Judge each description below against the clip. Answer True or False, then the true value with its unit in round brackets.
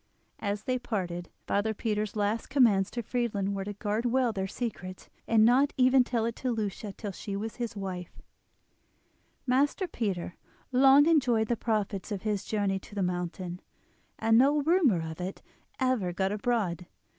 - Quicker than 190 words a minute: False (170 wpm)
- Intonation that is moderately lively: True (4.1 semitones)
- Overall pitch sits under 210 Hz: False (215 Hz)